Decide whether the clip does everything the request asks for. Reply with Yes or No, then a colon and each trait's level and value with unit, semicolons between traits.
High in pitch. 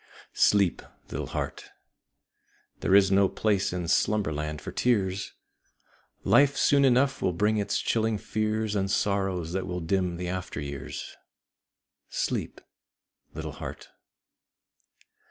No: very low, 95 Hz